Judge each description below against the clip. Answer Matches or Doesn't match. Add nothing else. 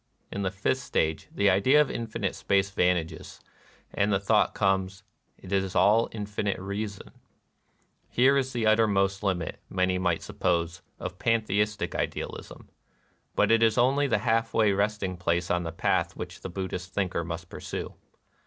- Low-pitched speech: Matches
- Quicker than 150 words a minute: Matches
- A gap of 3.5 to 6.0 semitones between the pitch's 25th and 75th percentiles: Doesn't match